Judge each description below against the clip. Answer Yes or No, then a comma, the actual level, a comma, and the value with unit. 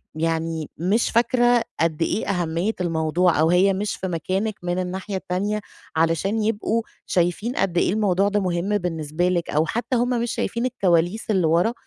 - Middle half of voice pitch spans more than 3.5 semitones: Yes, average, 4.0 semitones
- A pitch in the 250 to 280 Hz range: No, medium, 185 Hz